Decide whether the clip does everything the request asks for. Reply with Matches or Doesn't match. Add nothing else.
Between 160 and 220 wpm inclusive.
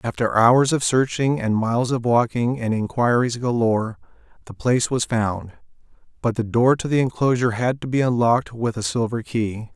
Matches